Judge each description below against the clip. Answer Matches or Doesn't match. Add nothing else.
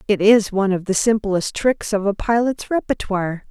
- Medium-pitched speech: Doesn't match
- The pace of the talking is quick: Doesn't match